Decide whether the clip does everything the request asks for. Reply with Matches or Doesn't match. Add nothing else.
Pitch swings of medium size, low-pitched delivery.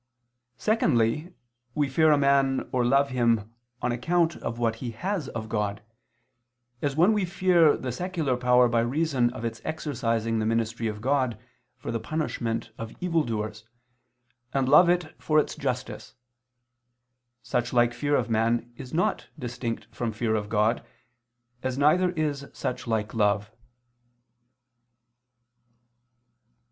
Matches